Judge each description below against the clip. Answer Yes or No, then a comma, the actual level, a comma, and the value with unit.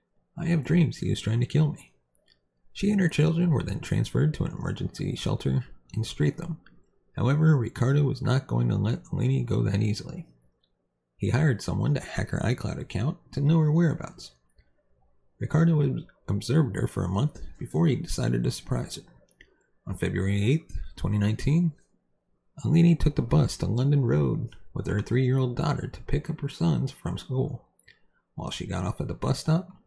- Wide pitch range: Yes, wide, 8.1 semitones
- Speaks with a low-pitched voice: Yes, low, 130 Hz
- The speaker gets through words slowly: No, average, 180 wpm